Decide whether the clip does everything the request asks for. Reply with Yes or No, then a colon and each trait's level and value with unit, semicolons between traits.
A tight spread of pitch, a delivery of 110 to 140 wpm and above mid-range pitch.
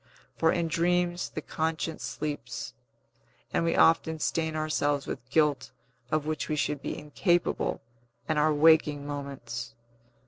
No: narrow, 2.0 semitones; slow, 135 wpm; medium, 155 Hz